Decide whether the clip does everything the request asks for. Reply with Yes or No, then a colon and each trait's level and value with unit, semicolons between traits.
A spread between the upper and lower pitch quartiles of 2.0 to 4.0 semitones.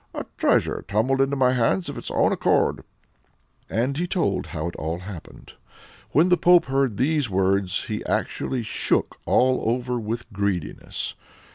No: wide, 5.6 semitones